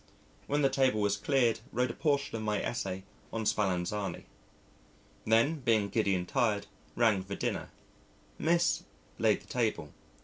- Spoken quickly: No, average, 145 wpm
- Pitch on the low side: Yes, low, 110 Hz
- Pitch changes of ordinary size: Yes, average, 4.4 semitones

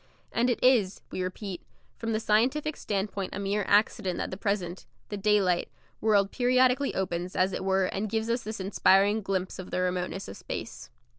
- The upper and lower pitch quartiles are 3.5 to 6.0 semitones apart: No, average, 2.9 semitones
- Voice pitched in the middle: No, high, 200 Hz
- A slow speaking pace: No, average, 180 wpm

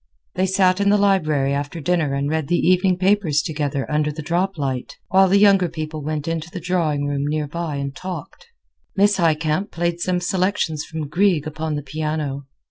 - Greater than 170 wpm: Yes, average, 185 wpm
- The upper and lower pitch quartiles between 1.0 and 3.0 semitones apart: No, average, 3.7 semitones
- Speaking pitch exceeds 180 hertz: No, medium, 160 Hz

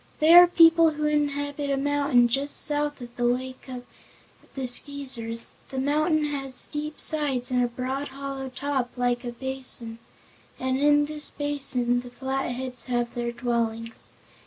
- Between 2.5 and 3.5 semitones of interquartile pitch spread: Yes, average, 2.9 semitones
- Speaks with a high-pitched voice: Yes, very high, 265 Hz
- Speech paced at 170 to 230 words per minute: No, average, 155 wpm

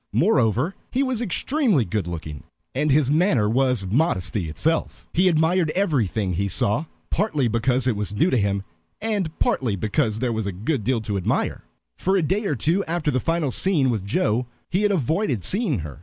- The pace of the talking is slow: No, average, 185 wpm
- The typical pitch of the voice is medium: No, low, 130 Hz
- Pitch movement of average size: No, wide, 8.5 semitones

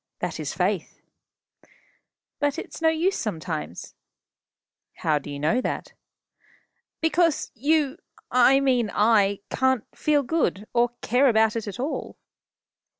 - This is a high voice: Yes, high, 245 Hz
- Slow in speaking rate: Yes, slow, 125 wpm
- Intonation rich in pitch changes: Yes, wide, 5.9 semitones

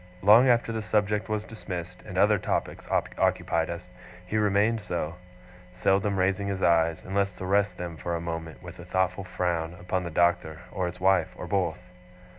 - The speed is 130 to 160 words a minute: No, average, 180 wpm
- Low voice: Yes, very low, 90 Hz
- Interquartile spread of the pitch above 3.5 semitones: No, average, 2.8 semitones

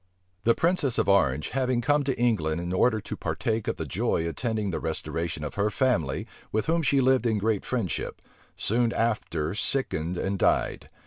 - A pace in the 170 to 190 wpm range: Yes, average, 180 wpm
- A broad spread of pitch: Yes, wide, 6.4 semitones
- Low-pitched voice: Yes, low, 110 Hz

